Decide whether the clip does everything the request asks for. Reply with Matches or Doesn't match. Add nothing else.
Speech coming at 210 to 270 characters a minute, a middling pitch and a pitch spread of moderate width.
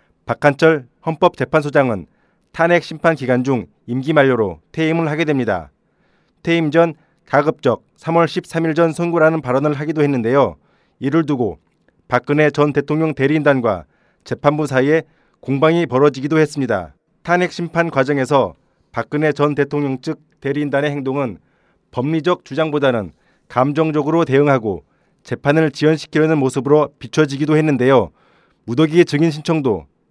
Doesn't match